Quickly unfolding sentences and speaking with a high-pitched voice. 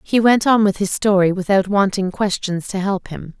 Yes: fast, 210 wpm; high, 195 Hz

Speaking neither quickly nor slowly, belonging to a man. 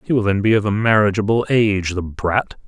No: fast, 225 wpm; male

